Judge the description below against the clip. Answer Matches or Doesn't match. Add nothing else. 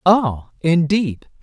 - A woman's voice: Matches